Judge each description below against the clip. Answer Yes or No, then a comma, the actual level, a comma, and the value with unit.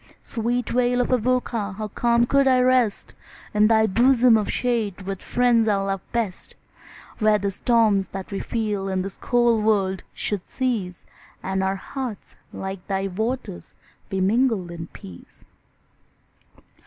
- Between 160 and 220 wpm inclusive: No, average, 150 wpm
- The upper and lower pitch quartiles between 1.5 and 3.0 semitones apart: No, average, 3.8 semitones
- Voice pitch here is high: Yes, high, 215 Hz